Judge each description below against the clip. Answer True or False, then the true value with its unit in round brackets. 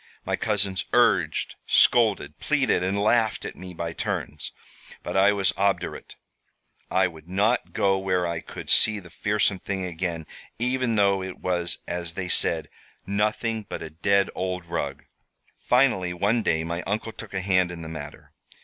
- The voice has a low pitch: True (95 Hz)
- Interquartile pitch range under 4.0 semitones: True (3.0 semitones)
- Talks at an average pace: True (165 wpm)